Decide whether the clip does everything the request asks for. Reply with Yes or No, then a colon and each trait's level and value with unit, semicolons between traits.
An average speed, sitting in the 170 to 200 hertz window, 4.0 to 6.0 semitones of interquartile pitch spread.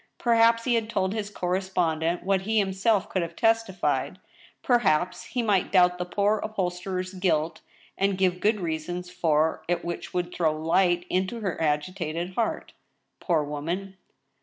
No: average, 150 wpm; medium, 185 Hz; average, 2.8 semitones